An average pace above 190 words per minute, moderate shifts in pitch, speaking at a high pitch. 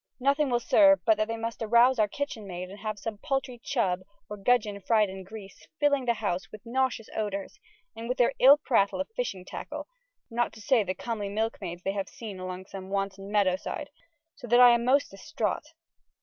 Yes: average, 200 wpm; average, 4.0 semitones; high, 220 Hz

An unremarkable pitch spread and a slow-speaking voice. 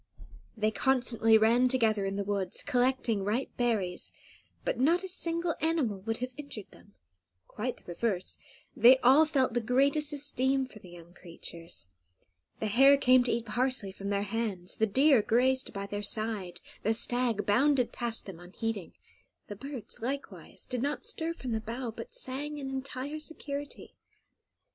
No: average, 4.5 semitones; average, 160 wpm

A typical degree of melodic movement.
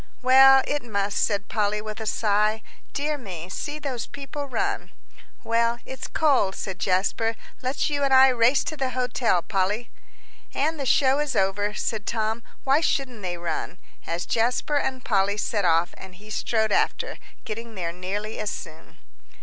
Yes: average, 4.9 semitones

